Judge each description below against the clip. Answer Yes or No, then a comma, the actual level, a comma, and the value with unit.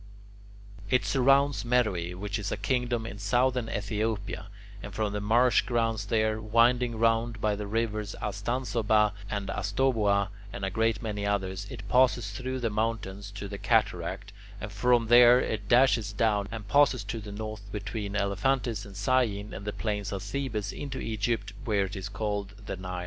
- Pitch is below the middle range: Yes, low, 105 Hz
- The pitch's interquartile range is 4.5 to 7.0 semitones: No, average, 2.7 semitones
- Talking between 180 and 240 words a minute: No, average, 170 wpm